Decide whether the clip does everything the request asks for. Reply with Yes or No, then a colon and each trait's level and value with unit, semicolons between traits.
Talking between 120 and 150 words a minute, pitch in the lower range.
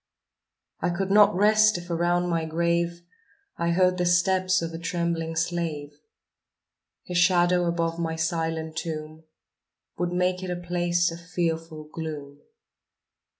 No: slow, 135 wpm; medium, 170 Hz